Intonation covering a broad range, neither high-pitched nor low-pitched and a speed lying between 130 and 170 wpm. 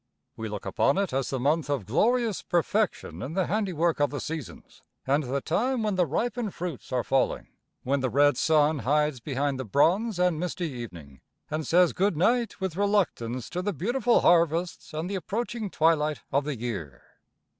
No: wide, 6.0 semitones; medium, 160 Hz; average, 180 wpm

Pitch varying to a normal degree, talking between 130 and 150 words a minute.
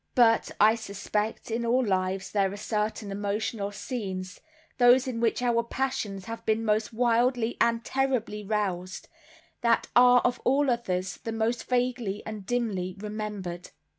Yes: average, 3.1 semitones; average, 145 wpm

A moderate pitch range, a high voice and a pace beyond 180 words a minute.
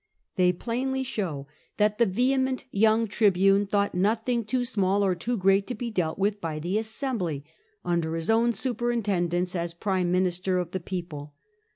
No: average, 4.3 semitones; high, 195 Hz; average, 165 wpm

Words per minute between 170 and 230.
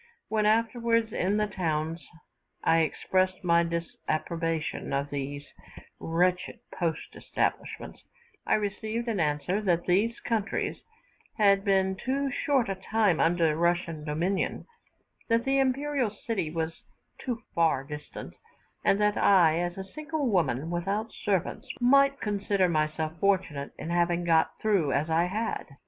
No: slow, 135 wpm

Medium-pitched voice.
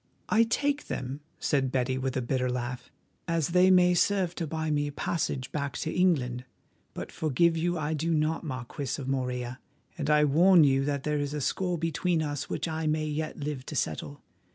Yes: medium, 150 Hz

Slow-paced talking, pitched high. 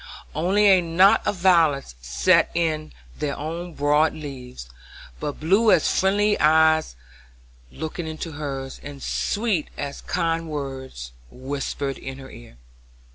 No: slow, 130 wpm; medium, 155 Hz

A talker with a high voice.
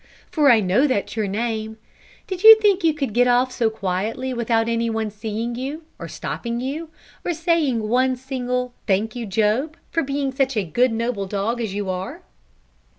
Yes: high, 240 Hz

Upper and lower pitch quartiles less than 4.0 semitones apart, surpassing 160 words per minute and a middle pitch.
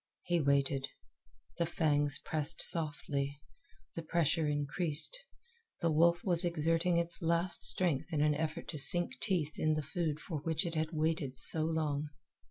No: narrow, 2.4 semitones; average, 155 wpm; medium, 155 Hz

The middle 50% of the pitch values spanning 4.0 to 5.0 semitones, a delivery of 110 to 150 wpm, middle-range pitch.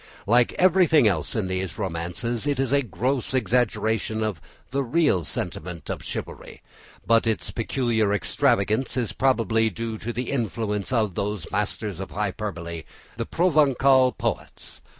No: average, 4.3 semitones; average, 140 wpm; low, 110 Hz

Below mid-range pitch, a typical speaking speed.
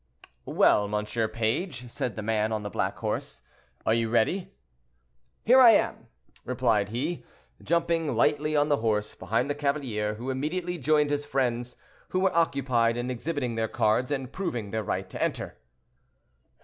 Yes: low, 125 Hz; average, 160 wpm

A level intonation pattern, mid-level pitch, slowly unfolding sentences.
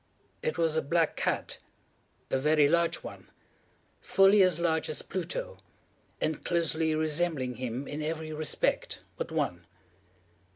Yes: narrow, 2.2 semitones; medium, 160 Hz; slow, 120 wpm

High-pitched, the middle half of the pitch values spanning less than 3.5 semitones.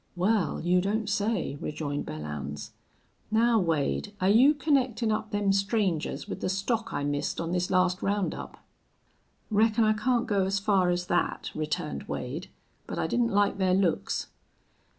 No: high, 195 Hz; average, 4.0 semitones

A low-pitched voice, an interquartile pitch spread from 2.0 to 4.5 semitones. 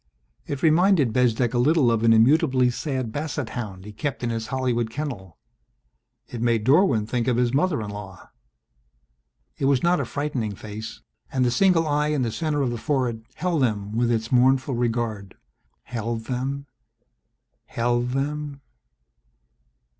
Yes: low, 125 Hz; average, 4.1 semitones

